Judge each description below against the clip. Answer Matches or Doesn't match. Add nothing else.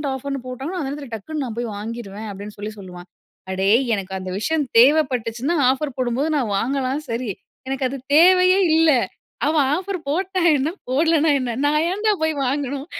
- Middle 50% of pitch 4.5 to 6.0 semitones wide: Matches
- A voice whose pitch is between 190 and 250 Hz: Doesn't match